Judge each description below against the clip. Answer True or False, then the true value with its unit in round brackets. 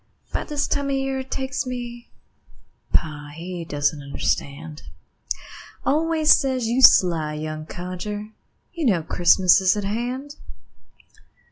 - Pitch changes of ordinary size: False (8.5 semitones)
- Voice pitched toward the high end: True (205 Hz)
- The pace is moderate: False (125 wpm)